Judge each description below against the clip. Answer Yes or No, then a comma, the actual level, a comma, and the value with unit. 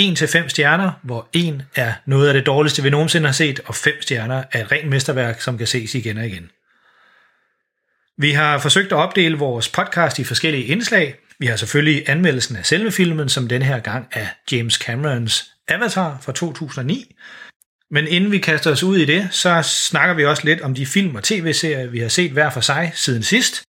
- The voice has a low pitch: No, medium, 150 Hz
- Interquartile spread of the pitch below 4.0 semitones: No, average, 4.4 semitones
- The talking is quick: No, average, 205 wpm